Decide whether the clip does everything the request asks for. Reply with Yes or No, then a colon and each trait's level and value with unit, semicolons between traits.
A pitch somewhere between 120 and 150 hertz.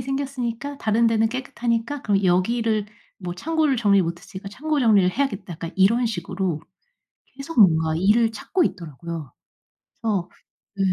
No: high, 215 Hz